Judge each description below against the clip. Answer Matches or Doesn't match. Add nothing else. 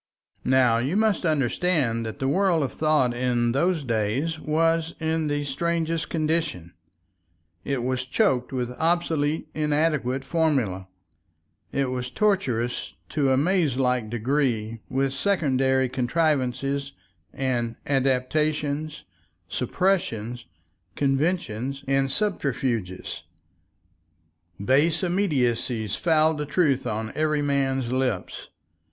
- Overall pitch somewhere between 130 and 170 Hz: Matches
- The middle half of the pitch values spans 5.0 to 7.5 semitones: Doesn't match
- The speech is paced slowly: Matches